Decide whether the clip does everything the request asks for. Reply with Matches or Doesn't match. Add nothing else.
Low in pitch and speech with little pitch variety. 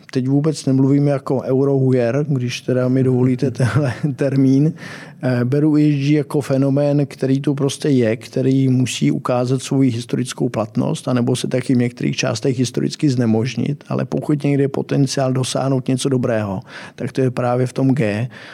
Matches